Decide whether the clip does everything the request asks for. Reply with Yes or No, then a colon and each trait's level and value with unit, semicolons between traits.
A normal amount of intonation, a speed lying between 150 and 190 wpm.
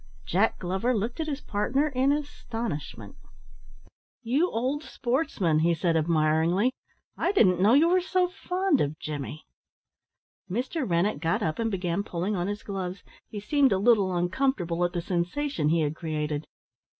No: wide, 7.8 semitones; average, 155 wpm